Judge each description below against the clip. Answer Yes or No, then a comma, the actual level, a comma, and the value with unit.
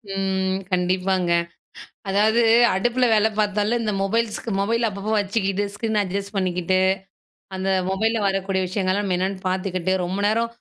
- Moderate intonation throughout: No, narrow, 2.3 semitones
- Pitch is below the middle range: No, high, 195 Hz